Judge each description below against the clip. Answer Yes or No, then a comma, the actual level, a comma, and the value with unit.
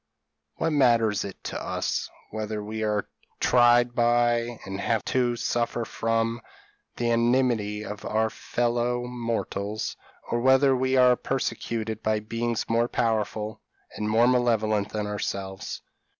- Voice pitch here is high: No, low, 115 Hz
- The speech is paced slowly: Yes, slow, 130 wpm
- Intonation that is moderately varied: No, narrow, 2.0 semitones